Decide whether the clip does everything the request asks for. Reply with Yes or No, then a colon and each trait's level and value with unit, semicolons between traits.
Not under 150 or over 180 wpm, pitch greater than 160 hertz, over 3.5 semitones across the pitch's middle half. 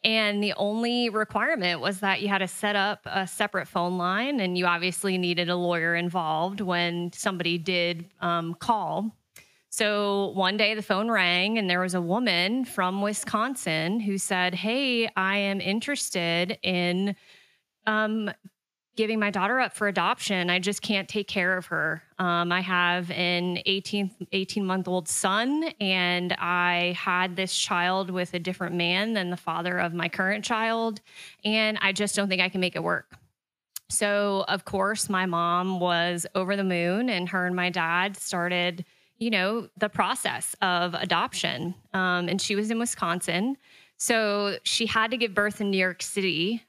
No: average, 170 wpm; high, 190 Hz; average, 2.8 semitones